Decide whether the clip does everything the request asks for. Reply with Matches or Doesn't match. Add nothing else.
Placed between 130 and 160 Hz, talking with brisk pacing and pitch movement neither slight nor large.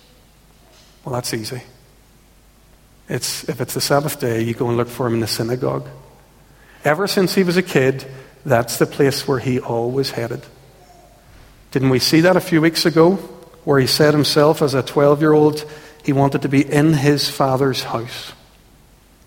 Doesn't match